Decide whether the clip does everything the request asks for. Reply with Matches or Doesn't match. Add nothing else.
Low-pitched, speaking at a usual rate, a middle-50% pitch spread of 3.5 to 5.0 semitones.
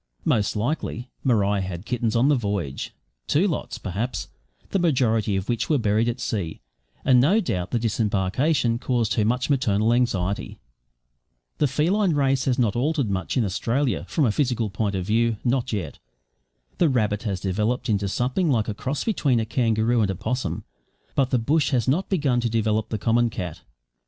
Matches